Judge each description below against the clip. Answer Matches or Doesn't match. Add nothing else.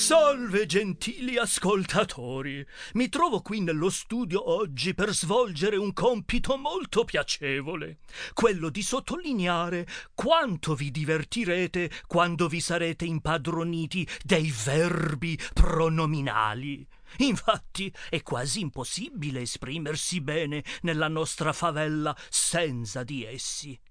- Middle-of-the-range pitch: Matches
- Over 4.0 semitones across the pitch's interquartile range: Matches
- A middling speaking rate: Doesn't match